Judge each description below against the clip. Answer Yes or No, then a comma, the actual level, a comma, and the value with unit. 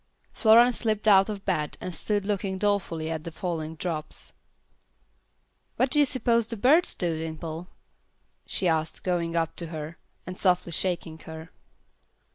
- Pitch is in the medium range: Yes, medium, 180 Hz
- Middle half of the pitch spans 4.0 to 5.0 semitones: Yes, average, 4.3 semitones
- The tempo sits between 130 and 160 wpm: Yes, average, 150 wpm